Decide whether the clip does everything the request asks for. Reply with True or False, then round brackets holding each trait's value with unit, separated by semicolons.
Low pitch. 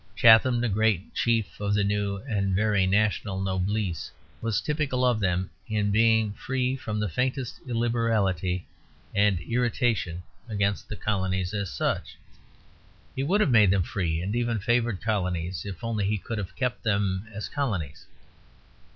True (105 Hz)